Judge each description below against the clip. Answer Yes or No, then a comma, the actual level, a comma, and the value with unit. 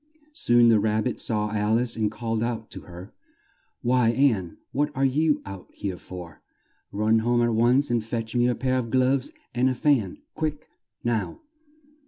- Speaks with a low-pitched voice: Yes, low, 120 Hz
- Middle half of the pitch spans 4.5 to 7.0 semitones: No, average, 2.9 semitones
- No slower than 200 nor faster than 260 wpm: No, average, 180 wpm